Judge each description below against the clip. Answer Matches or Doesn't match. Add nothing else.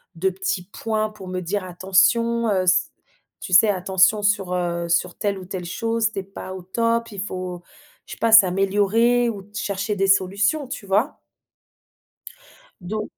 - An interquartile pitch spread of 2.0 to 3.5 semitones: Matches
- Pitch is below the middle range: Doesn't match